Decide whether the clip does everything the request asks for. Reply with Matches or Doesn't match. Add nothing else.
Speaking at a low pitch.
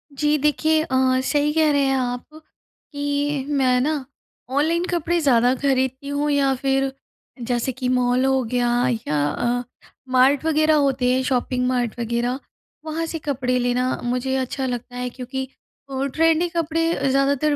Doesn't match